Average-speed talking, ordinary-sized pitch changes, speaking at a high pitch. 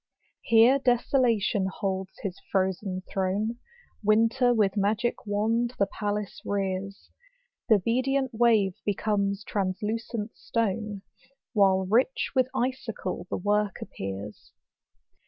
No: slow, 100 wpm; average, 3.1 semitones; high, 210 Hz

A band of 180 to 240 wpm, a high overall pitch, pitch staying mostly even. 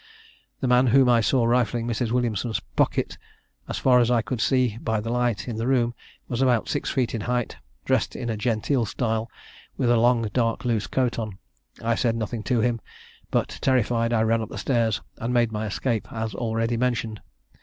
No: average, 195 wpm; low, 115 Hz; narrow, 1.7 semitones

